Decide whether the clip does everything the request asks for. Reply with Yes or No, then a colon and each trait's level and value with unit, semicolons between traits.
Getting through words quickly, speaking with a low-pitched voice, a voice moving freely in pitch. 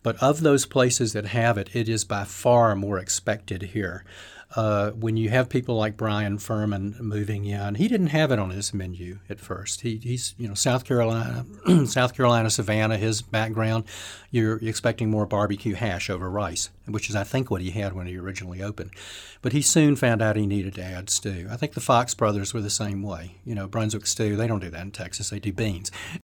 No: fast, 215 wpm; low, 105 Hz; average, 2.7 semitones